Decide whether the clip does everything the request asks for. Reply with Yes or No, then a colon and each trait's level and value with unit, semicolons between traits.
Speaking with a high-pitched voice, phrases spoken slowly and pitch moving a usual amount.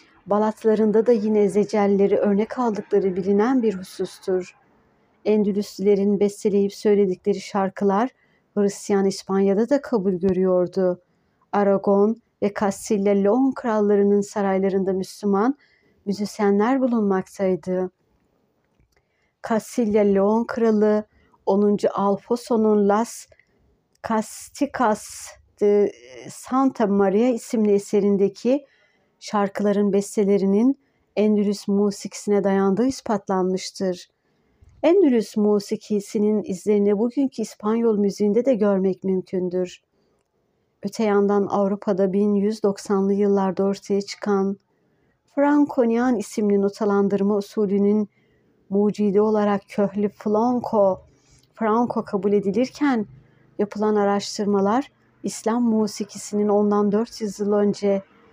No: high, 205 Hz; slow, 80 wpm; narrow, 1.6 semitones